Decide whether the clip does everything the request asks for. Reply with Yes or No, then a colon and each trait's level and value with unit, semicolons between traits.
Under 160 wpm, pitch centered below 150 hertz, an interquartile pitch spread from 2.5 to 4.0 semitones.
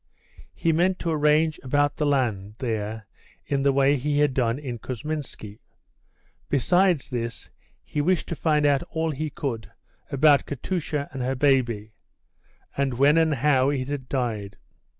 Yes: average, 150 wpm; medium, 140 Hz; average, 3.3 semitones